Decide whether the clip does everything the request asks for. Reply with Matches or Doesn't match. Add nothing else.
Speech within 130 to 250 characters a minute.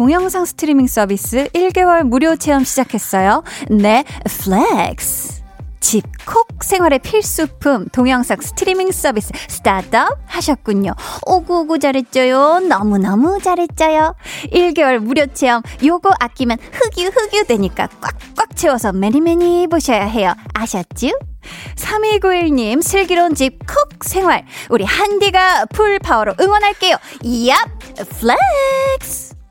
Doesn't match